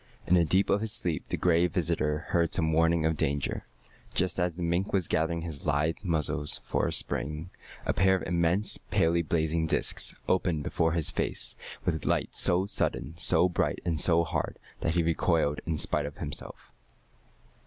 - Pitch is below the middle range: Yes, very low, 85 Hz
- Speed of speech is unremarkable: Yes, average, 185 wpm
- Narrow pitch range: Yes, narrow, 2.0 semitones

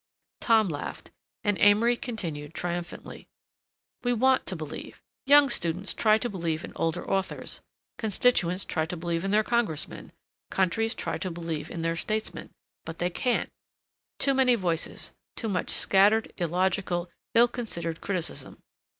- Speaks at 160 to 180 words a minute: No, average, 140 wpm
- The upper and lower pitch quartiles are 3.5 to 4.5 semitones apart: No, average, 4.9 semitones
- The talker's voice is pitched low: No, high, 190 Hz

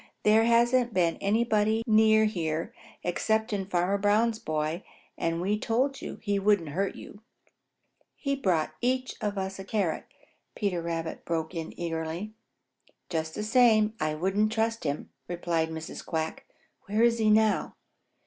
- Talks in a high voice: Yes, high, 200 Hz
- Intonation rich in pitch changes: No, average, 4.8 semitones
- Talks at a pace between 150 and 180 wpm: No, average, 140 wpm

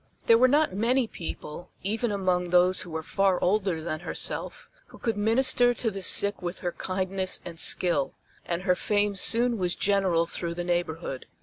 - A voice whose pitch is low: No, medium, 185 Hz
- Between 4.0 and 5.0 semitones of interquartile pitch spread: No, average, 3.5 semitones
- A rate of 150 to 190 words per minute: Yes, average, 180 wpm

